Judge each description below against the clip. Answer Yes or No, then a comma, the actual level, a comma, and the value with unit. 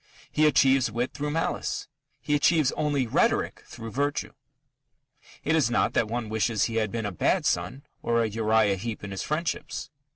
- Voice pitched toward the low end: Yes, low, 120 Hz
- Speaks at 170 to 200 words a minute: Yes, average, 175 wpm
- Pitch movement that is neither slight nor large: Yes, average, 4.7 semitones